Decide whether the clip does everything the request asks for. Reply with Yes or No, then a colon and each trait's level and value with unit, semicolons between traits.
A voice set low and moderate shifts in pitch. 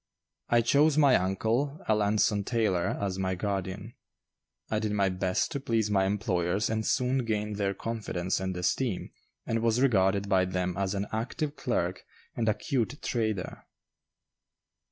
Yes: low, 105 Hz; average, 3.3 semitones